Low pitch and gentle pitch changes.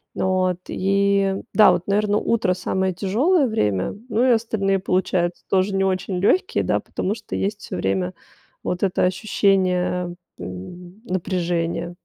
No: medium, 185 Hz; narrow, 2.1 semitones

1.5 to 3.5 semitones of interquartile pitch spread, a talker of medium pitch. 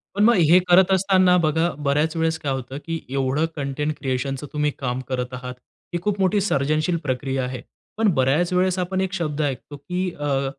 No: average, 5.0 semitones; medium, 150 Hz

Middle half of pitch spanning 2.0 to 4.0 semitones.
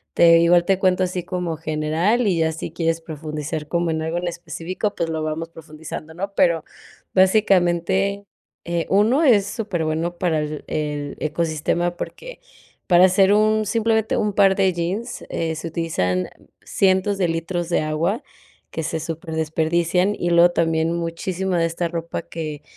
Yes: average, 2.8 semitones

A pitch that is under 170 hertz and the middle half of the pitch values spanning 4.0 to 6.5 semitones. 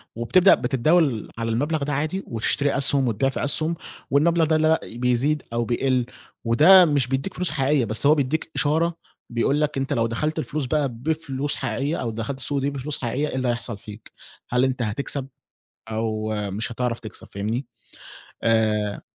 Yes: low, 135 Hz; average, 4.4 semitones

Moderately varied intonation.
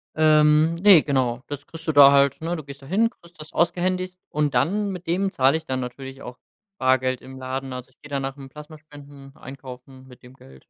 Yes: average, 3.6 semitones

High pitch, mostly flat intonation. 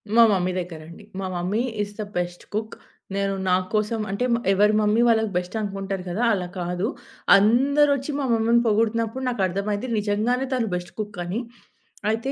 No: high, 210 Hz; average, 3.2 semitones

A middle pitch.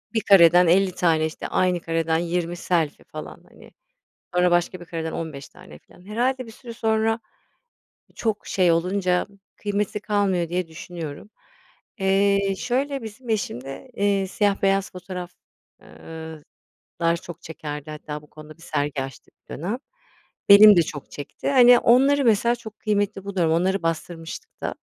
Yes: medium, 180 Hz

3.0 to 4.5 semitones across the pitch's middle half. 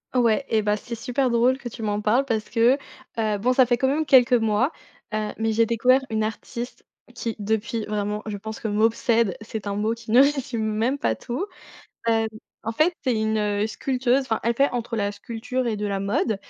No: narrow, 2.6 semitones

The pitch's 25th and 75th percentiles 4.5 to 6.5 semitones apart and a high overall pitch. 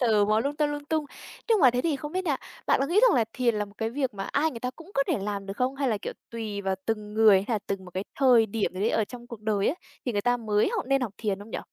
Yes: average, 4.8 semitones; high, 230 Hz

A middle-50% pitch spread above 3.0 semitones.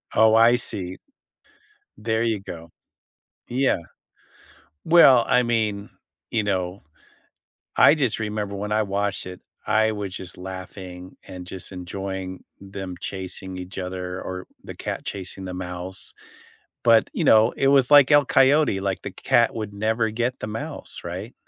Yes: average, 3.4 semitones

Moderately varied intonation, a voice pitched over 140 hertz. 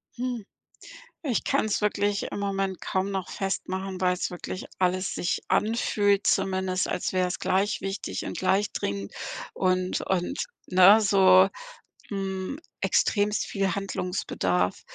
No: narrow, 1.6 semitones; high, 190 Hz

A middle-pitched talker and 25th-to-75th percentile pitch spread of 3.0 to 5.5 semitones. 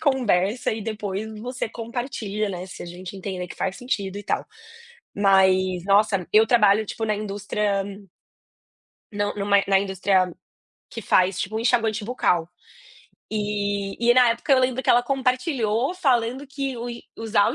No: high, 210 Hz; average, 3.4 semitones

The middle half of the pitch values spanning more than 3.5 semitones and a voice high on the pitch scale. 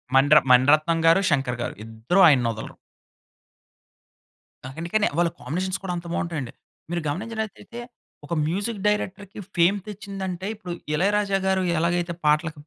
No: average, 4.4 semitones; medium, 175 Hz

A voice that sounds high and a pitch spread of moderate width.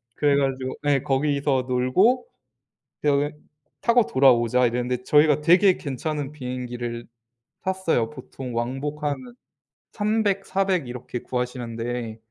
No: low, 135 Hz; average, 3.4 semitones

